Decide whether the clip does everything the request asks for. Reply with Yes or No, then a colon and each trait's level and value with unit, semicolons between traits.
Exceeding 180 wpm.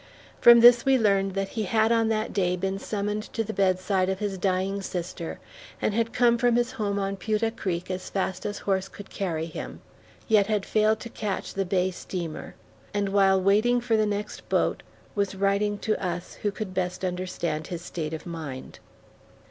Yes: average, 190 wpm